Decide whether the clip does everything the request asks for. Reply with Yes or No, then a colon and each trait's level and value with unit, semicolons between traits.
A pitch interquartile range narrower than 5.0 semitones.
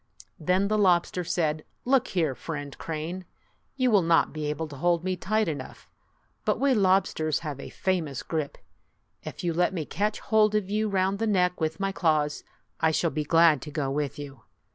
Yes: average, 4.2 semitones